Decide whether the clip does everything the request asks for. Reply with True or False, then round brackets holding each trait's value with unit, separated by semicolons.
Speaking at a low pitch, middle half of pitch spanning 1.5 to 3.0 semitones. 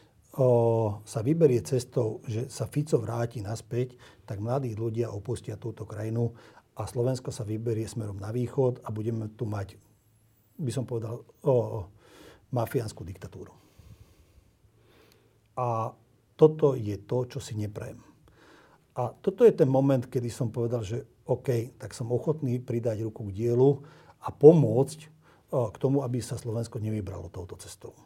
True (120 Hz; 2.7 semitones)